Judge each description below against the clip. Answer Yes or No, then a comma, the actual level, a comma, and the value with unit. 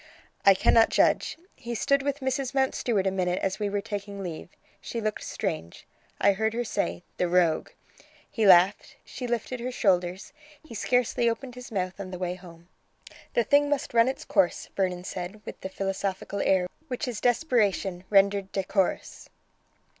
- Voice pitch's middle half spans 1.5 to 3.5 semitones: No, average, 4.4 semitones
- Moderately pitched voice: No, high, 200 Hz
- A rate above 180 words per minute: No, average, 170 wpm